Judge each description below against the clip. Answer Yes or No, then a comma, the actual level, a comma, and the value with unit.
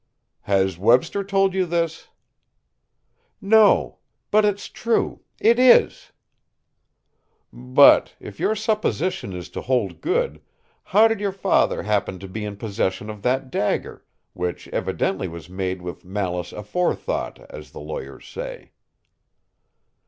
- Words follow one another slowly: Yes, slow, 125 wpm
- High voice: No, low, 125 Hz